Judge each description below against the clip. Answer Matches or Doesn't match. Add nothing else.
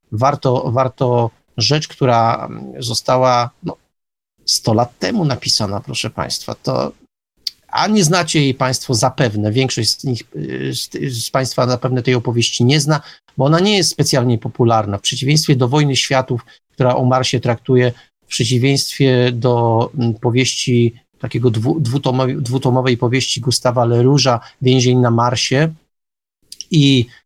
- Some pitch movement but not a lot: Doesn't match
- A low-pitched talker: Matches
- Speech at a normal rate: Matches